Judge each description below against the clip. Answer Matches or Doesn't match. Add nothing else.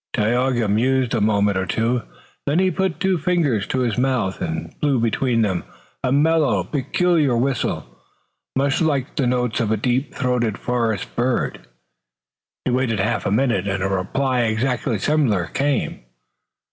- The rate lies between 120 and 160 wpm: Matches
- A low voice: Matches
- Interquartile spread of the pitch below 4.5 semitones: Matches